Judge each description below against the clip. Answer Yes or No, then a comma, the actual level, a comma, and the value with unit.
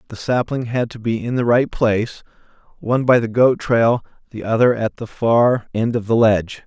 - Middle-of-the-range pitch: No, low, 115 Hz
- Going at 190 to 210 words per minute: Yes, average, 200 wpm